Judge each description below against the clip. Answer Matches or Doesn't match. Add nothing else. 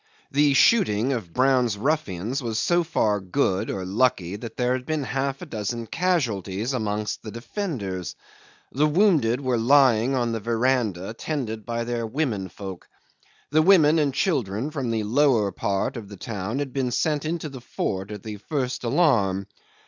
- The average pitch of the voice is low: Matches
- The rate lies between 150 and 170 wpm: Matches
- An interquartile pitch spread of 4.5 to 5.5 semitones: Matches